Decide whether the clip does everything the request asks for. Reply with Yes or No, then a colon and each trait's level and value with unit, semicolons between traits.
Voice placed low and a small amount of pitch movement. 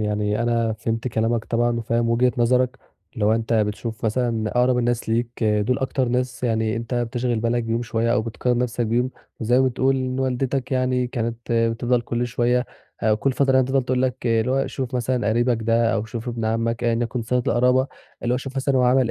Yes: low, 120 Hz; narrow, 1.8 semitones